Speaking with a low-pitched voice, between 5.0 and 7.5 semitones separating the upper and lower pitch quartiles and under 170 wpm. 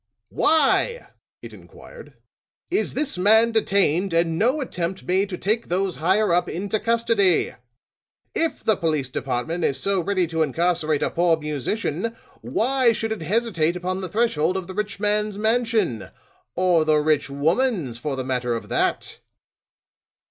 No: medium, 185 Hz; wide, 5.6 semitones; average, 150 wpm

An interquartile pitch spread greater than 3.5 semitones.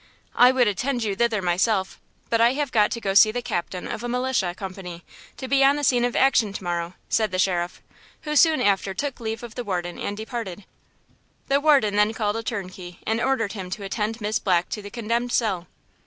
Yes: average, 4.2 semitones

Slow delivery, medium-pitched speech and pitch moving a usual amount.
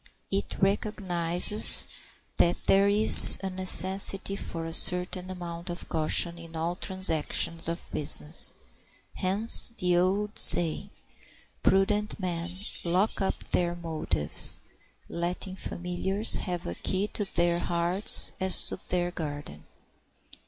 No: slow, 120 wpm; medium, 180 Hz; narrow, 2.2 semitones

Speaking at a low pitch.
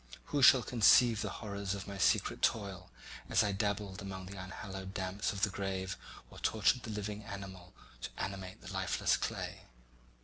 Yes: low, 100 Hz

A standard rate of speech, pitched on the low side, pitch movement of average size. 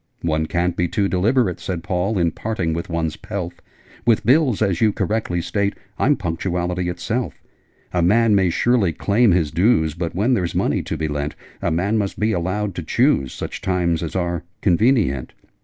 Yes: average, 180 wpm; very low, 90 Hz; average, 4.0 semitones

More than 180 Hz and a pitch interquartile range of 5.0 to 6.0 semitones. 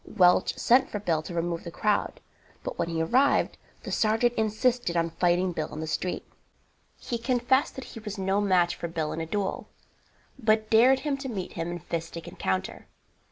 Yes: high, 190 Hz; wide, 5.6 semitones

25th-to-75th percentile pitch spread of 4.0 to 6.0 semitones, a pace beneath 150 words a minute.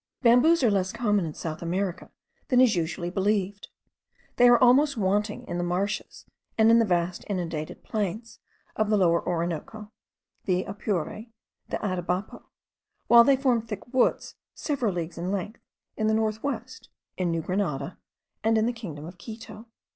No: average, 4.5 semitones; average, 165 wpm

